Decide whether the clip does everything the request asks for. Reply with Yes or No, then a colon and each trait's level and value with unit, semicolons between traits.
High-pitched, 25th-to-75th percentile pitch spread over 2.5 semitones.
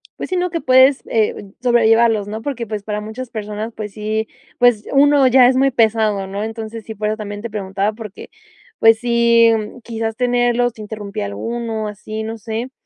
No: high, 225 Hz; narrow, 2.2 semitones